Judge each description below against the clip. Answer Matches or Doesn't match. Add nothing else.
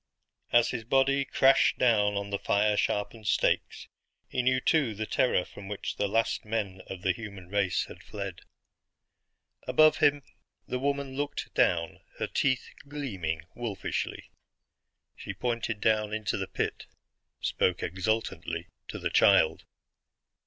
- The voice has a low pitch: Matches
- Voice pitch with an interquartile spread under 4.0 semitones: Doesn't match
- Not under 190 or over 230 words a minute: Doesn't match